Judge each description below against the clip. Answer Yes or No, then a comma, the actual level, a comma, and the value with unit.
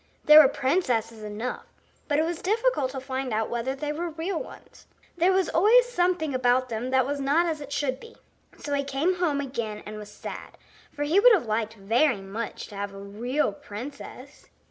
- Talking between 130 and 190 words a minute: No, average, 200 wpm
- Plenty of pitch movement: Yes, wide, 5.9 semitones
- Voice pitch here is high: Yes, very high, 275 Hz